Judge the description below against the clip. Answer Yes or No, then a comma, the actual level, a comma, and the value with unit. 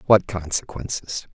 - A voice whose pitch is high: No, very low, 90 Hz